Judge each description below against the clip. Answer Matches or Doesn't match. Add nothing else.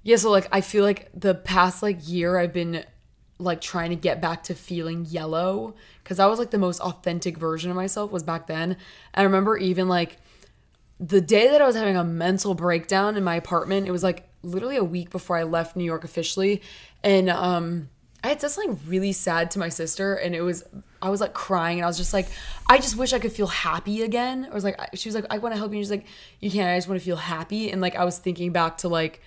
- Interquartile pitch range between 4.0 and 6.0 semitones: Doesn't match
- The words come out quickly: Matches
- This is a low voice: Doesn't match